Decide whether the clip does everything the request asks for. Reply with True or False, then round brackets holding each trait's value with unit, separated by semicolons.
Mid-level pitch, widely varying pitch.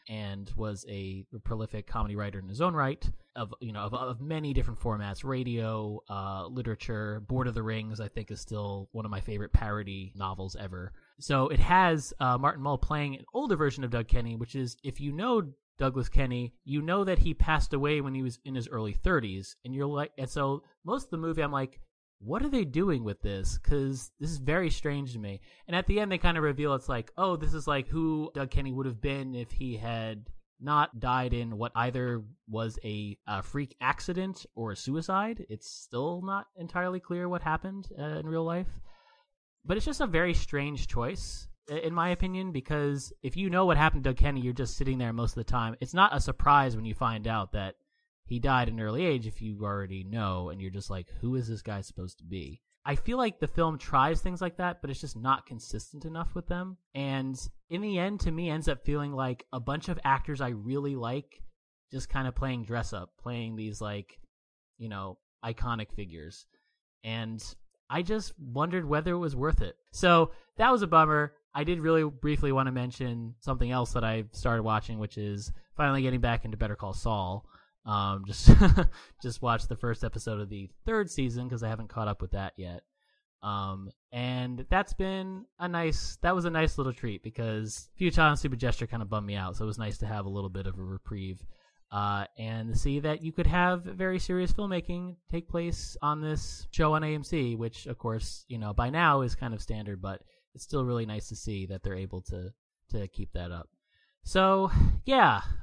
False (125 Hz; 6.3 semitones)